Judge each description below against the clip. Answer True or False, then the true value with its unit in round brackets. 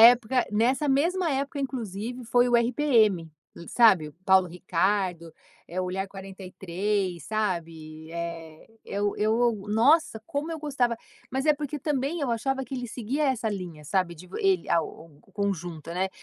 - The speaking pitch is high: True (210 Hz)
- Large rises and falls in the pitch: True (6.3 semitones)